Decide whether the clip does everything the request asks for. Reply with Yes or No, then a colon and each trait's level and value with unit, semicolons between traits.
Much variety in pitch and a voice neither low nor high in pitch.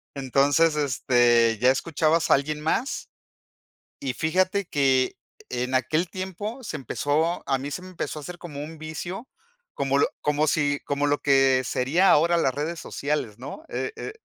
No: average, 3.7 semitones; medium, 145 Hz